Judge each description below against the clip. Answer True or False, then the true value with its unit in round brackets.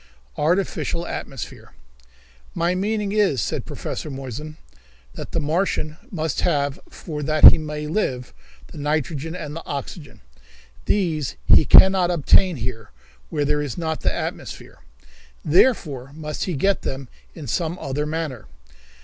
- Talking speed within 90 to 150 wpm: True (140 wpm)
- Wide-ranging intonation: False (3.5 semitones)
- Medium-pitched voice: True (155 Hz)